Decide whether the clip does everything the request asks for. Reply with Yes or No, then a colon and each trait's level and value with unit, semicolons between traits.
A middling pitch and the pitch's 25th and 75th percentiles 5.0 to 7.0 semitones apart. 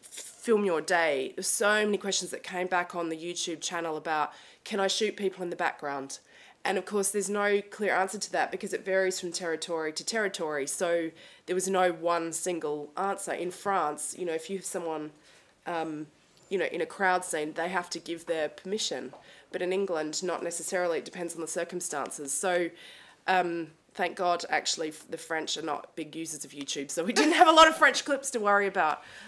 No: medium, 175 Hz; average, 3.2 semitones